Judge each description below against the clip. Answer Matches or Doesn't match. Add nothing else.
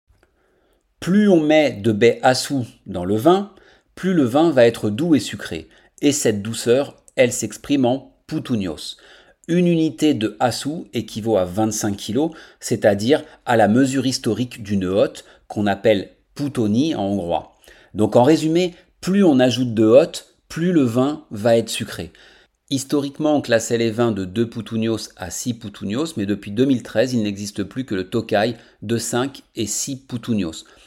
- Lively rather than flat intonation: Doesn't match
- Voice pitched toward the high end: Doesn't match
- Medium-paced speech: Matches